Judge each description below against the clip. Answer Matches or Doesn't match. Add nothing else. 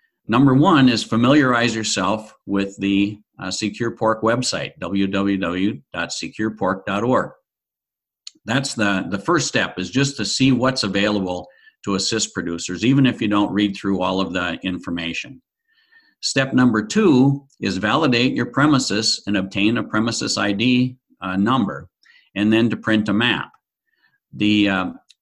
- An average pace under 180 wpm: Matches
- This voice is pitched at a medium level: Doesn't match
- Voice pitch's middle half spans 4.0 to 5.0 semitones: Matches